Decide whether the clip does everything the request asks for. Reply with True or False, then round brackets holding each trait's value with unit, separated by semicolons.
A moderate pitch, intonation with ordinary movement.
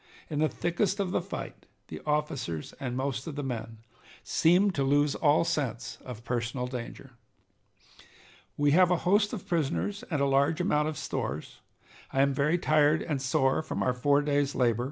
True (145 Hz; 3.9 semitones)